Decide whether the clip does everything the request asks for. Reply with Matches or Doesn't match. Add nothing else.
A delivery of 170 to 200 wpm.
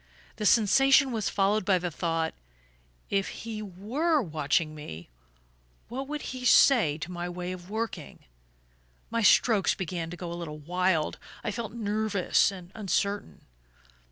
Doesn't match